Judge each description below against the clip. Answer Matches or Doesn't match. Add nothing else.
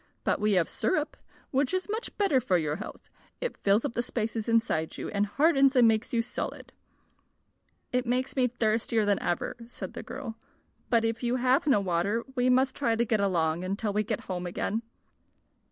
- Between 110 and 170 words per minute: Doesn't match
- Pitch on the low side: Doesn't match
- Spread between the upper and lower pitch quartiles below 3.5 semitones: Doesn't match